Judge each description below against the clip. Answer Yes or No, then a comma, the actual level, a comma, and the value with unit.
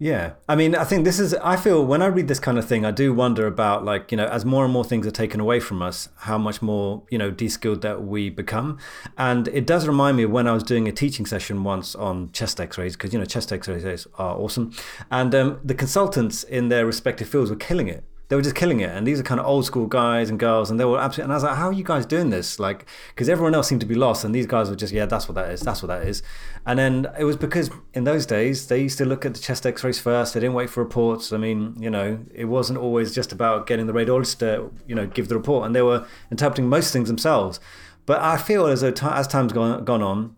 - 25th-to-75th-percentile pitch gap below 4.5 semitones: Yes, average, 3.9 semitones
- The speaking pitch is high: No, low, 120 Hz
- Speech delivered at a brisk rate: Yes, fast, 280 wpm